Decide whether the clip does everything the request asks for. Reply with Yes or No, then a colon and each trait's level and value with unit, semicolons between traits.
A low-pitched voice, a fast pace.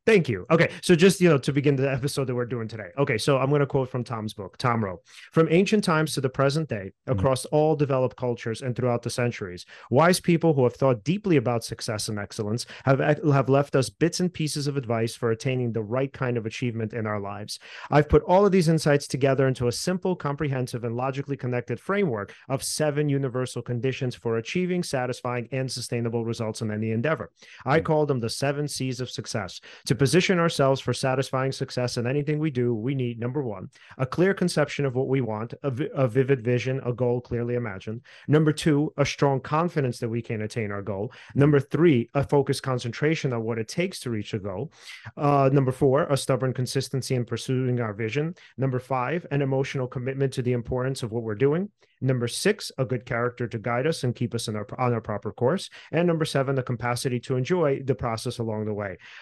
Yes: low, 130 Hz; fast, 215 wpm